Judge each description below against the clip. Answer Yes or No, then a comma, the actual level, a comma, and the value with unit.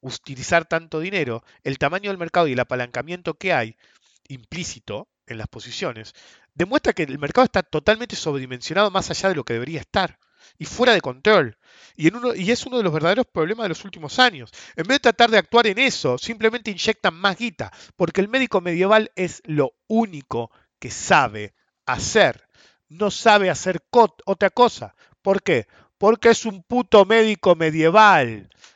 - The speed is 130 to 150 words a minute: No, average, 175 wpm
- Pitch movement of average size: No, wide, 6.2 semitones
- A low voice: No, high, 190 Hz